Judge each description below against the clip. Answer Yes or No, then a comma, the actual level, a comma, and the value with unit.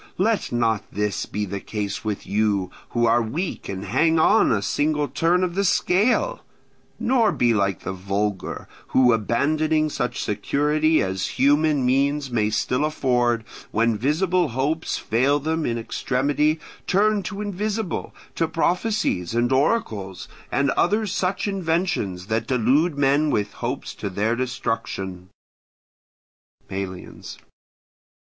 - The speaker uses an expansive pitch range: Yes, wide, 7.2 semitones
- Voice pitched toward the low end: Yes, low, 130 Hz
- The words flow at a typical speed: No, slow, 130 wpm